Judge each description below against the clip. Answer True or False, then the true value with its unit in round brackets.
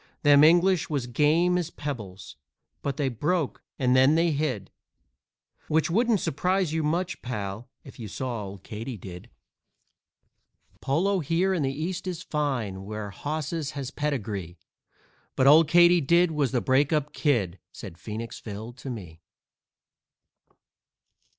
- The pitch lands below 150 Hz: True (140 Hz)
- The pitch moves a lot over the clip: True (6.3 semitones)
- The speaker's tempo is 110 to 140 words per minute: True (135 wpm)